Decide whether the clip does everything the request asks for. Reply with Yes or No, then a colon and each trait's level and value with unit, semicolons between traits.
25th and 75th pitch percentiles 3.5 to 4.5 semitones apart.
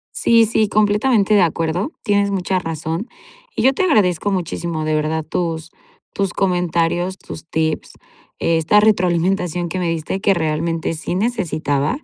Yes: average, 3.8 semitones